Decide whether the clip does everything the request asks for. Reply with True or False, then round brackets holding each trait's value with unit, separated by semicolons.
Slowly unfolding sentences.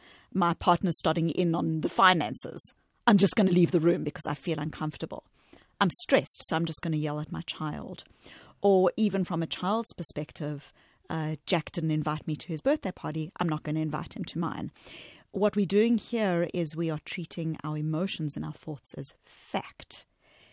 False (195 wpm)